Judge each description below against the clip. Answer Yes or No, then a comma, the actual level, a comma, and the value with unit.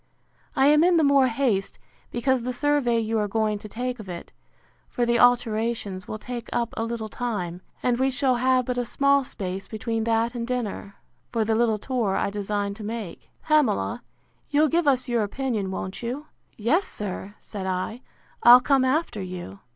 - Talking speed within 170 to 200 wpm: Yes, average, 180 wpm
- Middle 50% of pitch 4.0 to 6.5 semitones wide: No, average, 3.5 semitones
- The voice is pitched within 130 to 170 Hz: No, high, 235 Hz